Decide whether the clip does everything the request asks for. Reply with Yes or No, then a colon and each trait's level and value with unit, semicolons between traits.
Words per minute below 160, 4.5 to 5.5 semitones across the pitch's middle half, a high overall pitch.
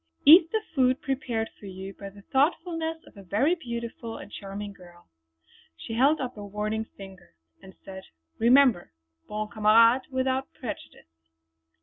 Yes: average, 145 wpm; average, 5.1 semitones; high, 225 Hz